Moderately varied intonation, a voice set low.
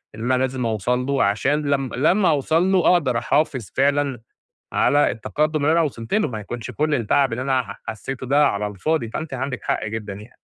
Yes: average, 4.4 semitones; low, 130 Hz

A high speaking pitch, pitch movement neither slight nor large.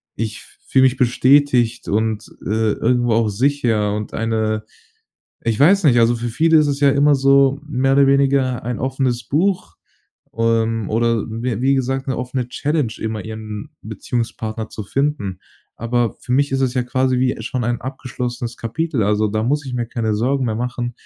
No: low, 120 Hz; average, 3.3 semitones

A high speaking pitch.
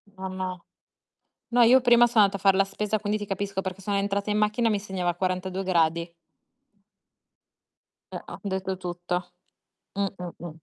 Yes: high, 195 Hz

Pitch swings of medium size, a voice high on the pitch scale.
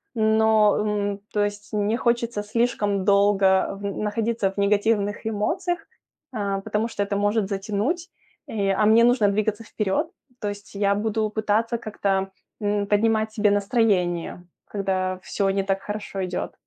No: narrow, 1.6 semitones; high, 205 Hz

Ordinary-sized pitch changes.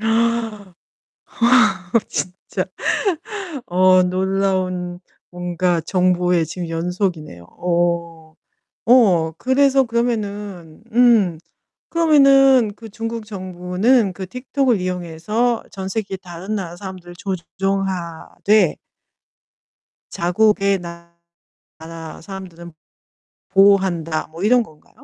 Yes: average, 3.9 semitones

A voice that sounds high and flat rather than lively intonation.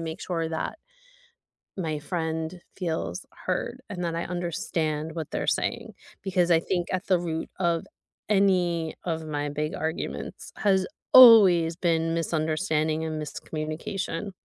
No: medium, 165 Hz; narrow, 2.3 semitones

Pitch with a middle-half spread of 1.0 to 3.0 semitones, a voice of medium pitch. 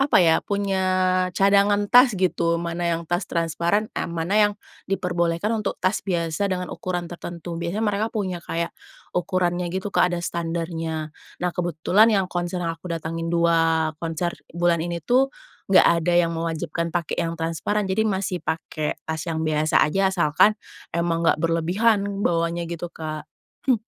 Yes: narrow, 2.5 semitones; medium, 175 Hz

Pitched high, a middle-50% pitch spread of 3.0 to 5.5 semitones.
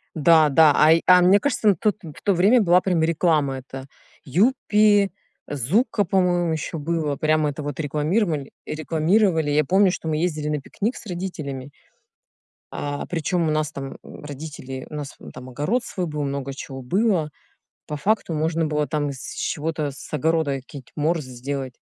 No: medium, 155 Hz; average, 3.7 semitones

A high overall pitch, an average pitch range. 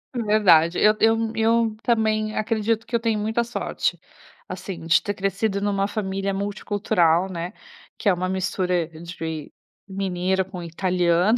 Yes: high, 195 Hz; average, 3.3 semitones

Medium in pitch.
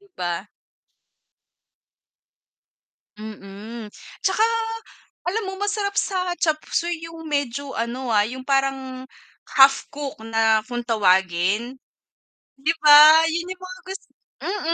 No: very high, 270 Hz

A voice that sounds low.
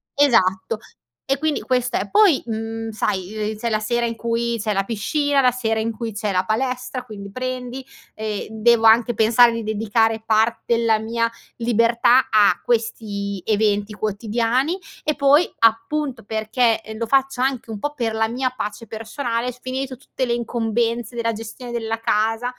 No: high, 230 Hz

